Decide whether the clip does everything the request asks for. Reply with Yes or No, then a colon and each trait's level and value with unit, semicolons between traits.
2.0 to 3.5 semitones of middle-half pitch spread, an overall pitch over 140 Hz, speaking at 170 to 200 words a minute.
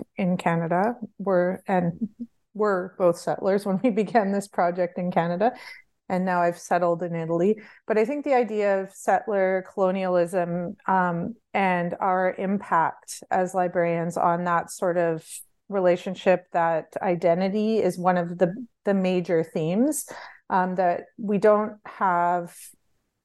No: average, 2.8 semitones; medium, 185 Hz; slow, 135 wpm